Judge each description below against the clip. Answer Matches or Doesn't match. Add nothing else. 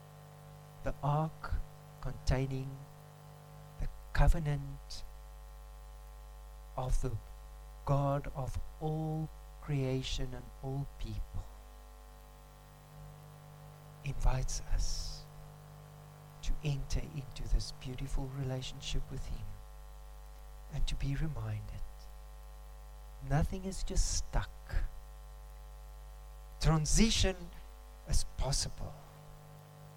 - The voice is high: Doesn't match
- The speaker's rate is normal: Doesn't match